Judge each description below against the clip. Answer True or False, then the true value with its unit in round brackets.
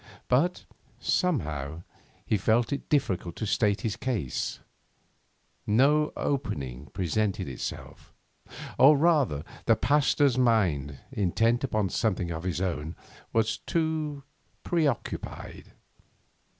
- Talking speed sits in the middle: False (100 wpm)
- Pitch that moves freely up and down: True (8.2 semitones)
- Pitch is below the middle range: True (110 Hz)